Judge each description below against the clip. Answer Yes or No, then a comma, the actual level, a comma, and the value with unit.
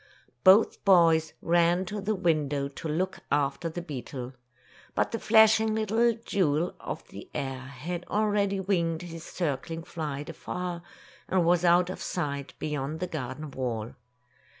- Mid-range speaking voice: Yes, medium, 170 Hz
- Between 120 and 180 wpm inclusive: Yes, average, 145 wpm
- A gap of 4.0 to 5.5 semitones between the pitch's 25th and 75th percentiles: Yes, average, 4.4 semitones